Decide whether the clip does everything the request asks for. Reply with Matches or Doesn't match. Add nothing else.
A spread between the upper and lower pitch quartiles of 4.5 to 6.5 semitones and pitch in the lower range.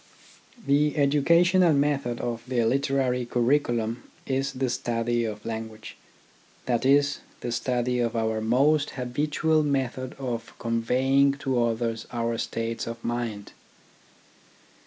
Doesn't match